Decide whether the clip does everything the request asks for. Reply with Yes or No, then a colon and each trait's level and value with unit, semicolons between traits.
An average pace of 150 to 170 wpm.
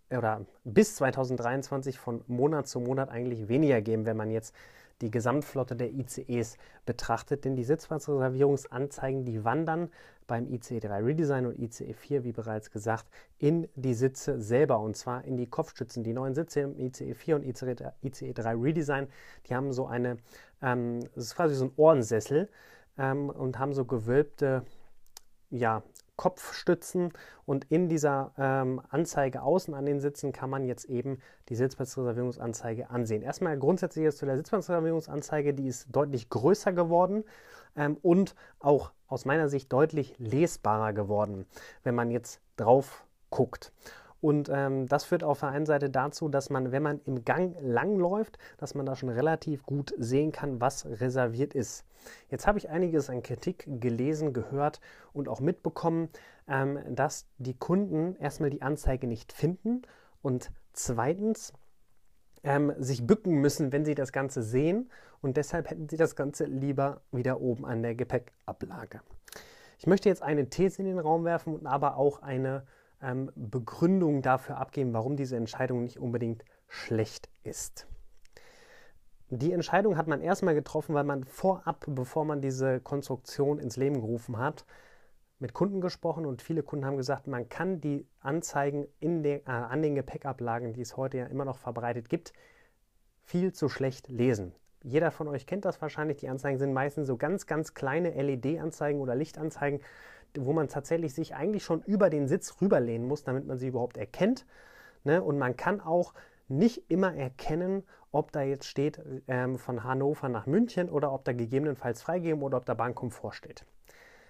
Yes: average, 165 wpm